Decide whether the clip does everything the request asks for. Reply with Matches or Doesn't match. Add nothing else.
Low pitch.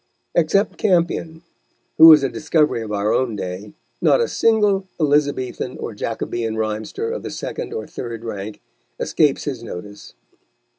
Matches